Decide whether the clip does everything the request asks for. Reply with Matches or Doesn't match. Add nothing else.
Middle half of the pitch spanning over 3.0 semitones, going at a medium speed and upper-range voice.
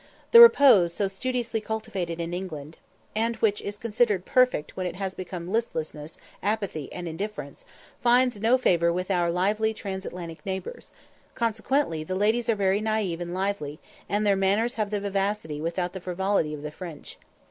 Matches